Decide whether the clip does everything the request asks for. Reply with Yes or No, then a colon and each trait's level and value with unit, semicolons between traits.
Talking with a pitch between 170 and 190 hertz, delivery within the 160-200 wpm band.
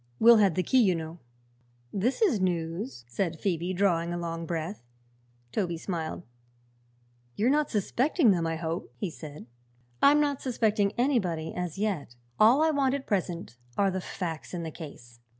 Yes: medium, 185 Hz; average, 165 wpm